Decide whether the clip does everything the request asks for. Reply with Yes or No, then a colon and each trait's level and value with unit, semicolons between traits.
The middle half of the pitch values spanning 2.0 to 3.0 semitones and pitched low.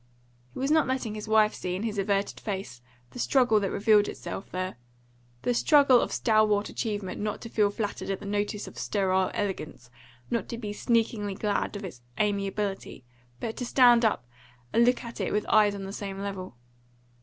No: narrow, 2.6 semitones; high, 210 Hz